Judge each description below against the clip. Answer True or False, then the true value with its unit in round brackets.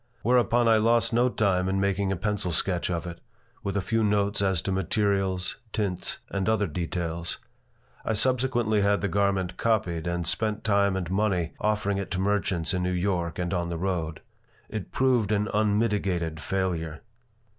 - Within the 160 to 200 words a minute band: True (170 wpm)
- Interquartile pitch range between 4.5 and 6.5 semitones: False (3.0 semitones)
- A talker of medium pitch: False (100 Hz)